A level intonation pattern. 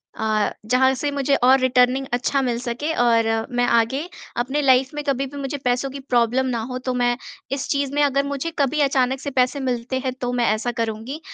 Yes: narrow, 2.1 semitones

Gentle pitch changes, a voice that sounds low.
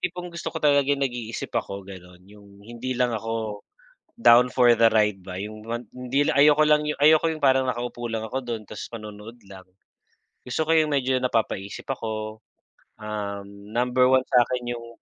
No: average, 3.8 semitones; low, 120 Hz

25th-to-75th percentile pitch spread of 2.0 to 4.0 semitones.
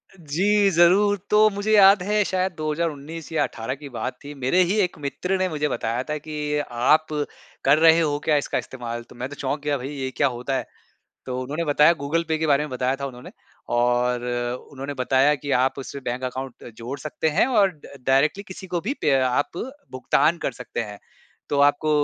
No: average, 4.5 semitones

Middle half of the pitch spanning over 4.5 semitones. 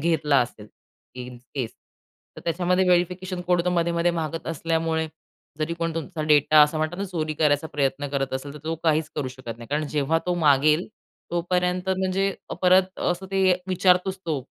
No: average, 3.4 semitones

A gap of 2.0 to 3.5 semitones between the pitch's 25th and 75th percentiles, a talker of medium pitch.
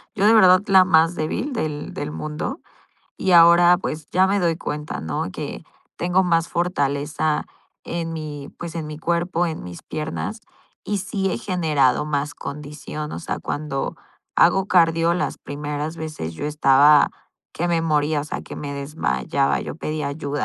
Yes: average, 3.0 semitones; medium, 155 Hz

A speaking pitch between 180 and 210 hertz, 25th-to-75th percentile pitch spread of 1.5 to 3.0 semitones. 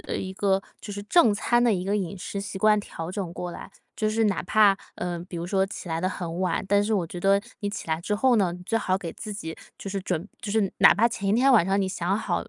Yes: high, 195 Hz; average, 2.7 semitones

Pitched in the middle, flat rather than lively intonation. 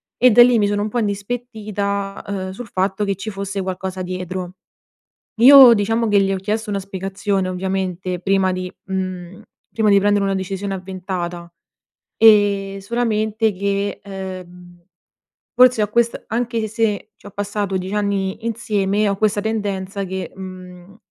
No: high, 200 Hz; narrow, 2.1 semitones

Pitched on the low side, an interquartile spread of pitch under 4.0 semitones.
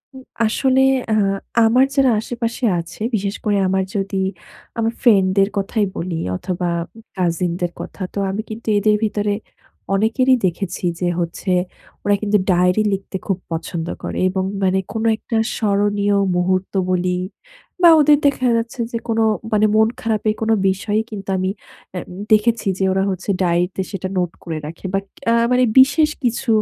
No: high, 205 Hz; average, 3.3 semitones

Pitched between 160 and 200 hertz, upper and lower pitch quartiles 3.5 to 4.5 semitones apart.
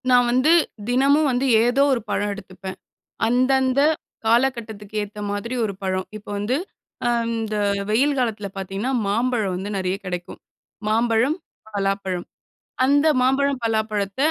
No: high, 225 Hz; average, 4.2 semitones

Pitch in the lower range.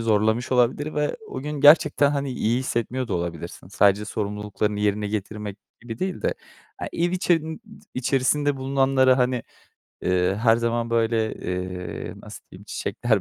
Yes: low, 115 Hz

